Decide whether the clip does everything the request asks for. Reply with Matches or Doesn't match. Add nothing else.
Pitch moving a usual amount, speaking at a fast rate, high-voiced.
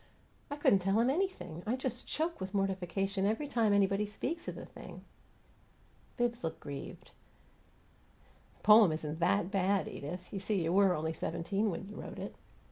Doesn't match